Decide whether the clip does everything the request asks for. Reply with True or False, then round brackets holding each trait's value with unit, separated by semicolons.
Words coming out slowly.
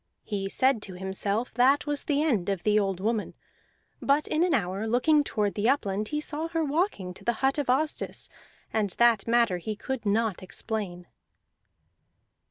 False (175 wpm)